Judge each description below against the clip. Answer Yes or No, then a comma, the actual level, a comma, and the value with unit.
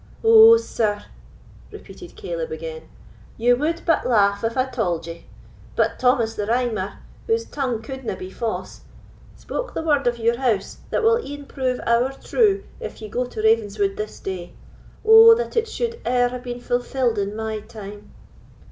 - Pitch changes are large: Yes, wide, 7.2 semitones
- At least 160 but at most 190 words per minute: Yes, average, 165 wpm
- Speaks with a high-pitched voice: Yes, high, 245 Hz